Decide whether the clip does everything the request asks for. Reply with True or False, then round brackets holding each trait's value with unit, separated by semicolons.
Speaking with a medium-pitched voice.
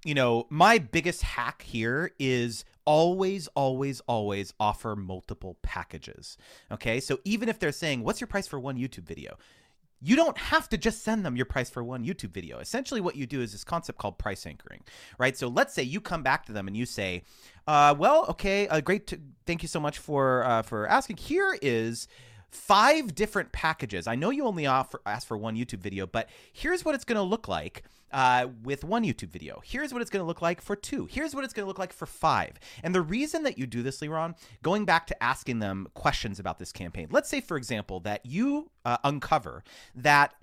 True (145 Hz)